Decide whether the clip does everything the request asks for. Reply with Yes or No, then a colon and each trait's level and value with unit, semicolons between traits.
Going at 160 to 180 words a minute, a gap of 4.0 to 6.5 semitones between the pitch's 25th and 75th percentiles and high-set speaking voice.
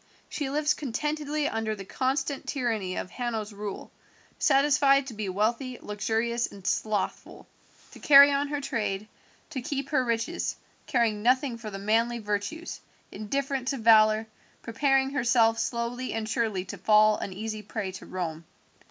No: average, 150 wpm; average, 4.3 semitones; high, 230 Hz